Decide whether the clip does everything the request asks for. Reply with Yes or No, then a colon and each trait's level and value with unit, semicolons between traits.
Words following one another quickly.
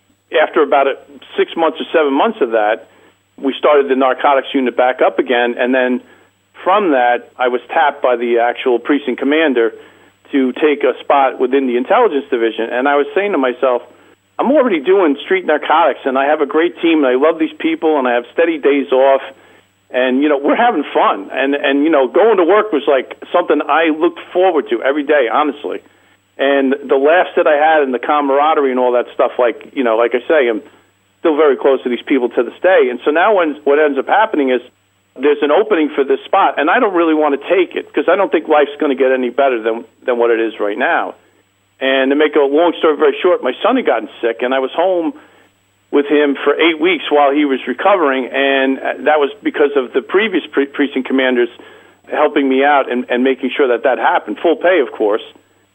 Yes: fast, 220 wpm